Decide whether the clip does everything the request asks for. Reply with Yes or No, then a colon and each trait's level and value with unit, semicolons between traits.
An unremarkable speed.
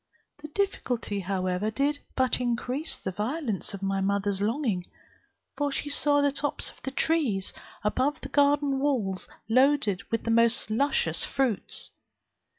Yes: average, 145 wpm